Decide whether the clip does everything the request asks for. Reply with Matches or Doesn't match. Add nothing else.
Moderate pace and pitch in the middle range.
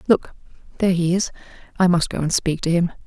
Matches